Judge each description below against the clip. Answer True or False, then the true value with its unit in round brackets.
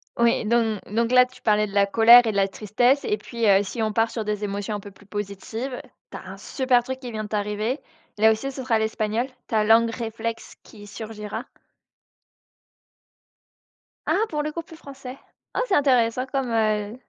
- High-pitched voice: True (225 Hz)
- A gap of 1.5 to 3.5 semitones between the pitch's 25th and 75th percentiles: True (3.0 semitones)